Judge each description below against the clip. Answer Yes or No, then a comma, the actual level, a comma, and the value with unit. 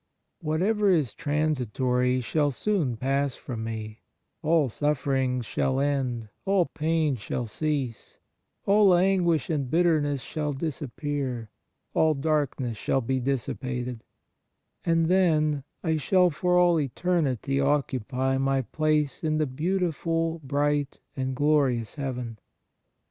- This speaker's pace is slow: Yes, slow, 120 wpm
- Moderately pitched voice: Yes, medium, 145 Hz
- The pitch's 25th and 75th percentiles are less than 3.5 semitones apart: No, average, 3.8 semitones